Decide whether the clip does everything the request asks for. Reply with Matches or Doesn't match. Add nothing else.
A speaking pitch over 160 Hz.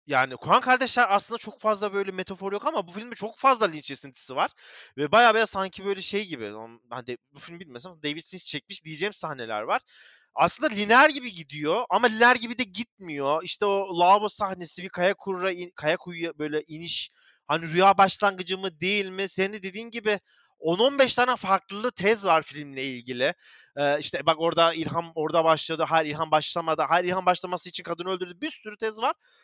Matches